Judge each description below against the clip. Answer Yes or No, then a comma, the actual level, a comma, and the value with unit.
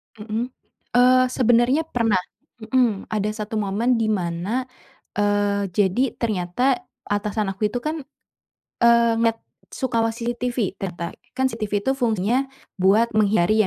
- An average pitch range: Yes, average, 3.1 semitones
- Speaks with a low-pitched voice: No, high, 225 Hz